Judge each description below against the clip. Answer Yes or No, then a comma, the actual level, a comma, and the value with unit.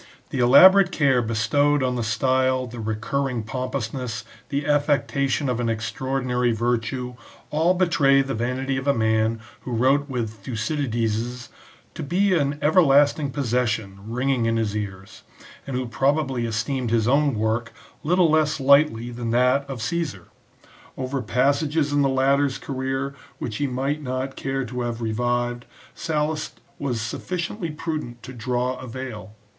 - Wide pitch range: No, average, 3.3 semitones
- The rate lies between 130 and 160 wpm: Yes, average, 150 wpm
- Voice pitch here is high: No, low, 130 Hz